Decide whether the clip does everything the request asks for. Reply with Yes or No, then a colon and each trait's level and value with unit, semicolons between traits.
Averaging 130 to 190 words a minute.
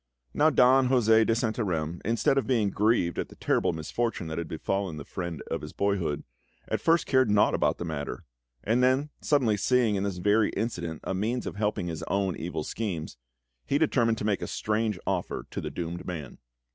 No: average, 200 wpm